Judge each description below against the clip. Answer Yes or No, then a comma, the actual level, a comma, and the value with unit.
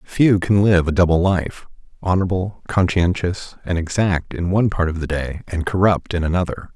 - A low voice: Yes, very low, 90 Hz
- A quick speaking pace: No, average, 170 wpm